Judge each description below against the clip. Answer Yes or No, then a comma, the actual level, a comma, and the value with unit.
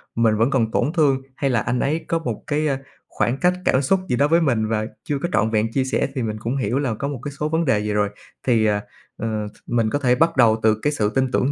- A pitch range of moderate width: Yes, average, 4.5 semitones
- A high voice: No, low, 125 Hz